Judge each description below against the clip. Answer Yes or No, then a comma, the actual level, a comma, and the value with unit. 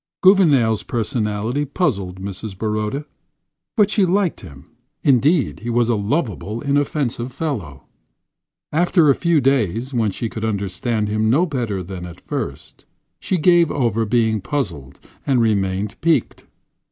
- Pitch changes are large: Yes, wide, 5.9 semitones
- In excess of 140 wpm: No, slow, 135 wpm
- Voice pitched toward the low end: Yes, low, 115 Hz